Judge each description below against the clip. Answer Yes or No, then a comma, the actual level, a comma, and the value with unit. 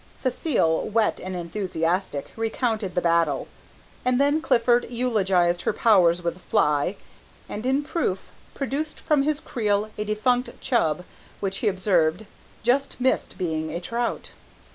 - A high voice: Yes, high, 210 Hz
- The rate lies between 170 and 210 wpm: No, average, 140 wpm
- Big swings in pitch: Yes, wide, 5.9 semitones